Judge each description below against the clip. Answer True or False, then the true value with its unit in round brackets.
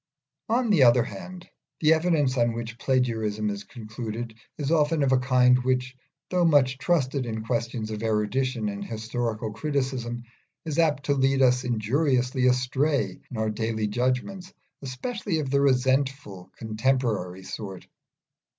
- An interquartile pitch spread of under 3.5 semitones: False (3.8 semitones)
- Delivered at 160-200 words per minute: False (140 wpm)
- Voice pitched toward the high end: False (125 Hz)